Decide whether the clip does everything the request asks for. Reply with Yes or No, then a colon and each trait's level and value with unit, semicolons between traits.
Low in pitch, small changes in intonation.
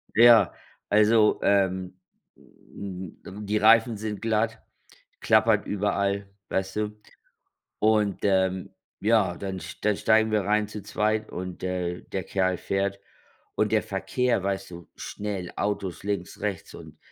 Yes: low, 100 Hz; narrow, 2.1 semitones